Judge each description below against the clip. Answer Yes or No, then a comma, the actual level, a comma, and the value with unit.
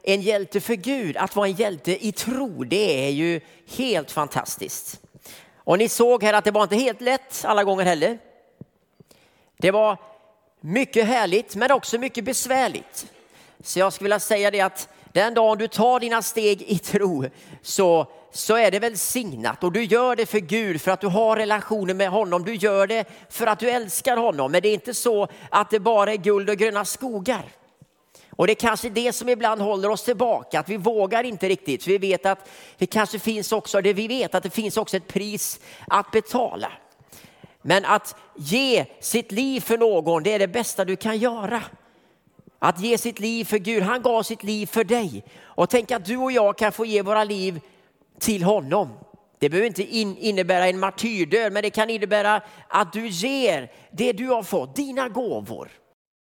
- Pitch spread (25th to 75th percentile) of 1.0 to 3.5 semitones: Yes, average, 2.8 semitones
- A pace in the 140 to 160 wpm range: No, fast, 195 wpm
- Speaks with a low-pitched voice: No, high, 215 Hz